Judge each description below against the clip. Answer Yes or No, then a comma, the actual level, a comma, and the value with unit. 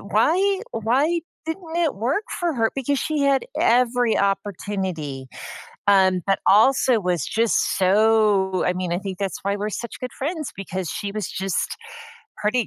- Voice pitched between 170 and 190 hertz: No, high, 215 Hz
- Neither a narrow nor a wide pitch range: No, wide, 5.7 semitones